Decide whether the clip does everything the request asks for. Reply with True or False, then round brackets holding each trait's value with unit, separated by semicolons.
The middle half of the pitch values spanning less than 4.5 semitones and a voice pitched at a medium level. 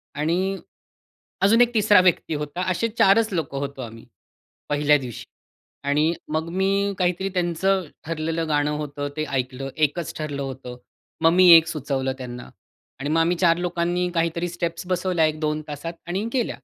True (3.8 semitones; 165 Hz)